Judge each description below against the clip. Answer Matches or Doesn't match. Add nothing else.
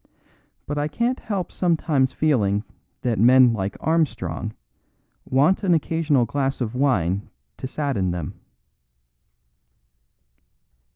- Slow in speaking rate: Matches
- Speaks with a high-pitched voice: Doesn't match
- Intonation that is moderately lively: Doesn't match